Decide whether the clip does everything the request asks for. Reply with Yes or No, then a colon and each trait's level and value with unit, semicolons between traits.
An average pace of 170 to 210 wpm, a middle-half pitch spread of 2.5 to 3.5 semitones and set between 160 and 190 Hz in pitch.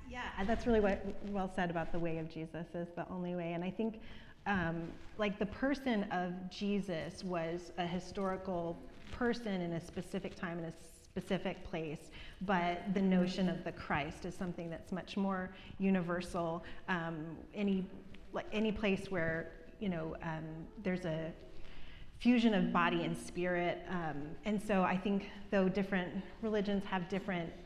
No: average, 160 wpm; average, 2.8 semitones; medium, 185 Hz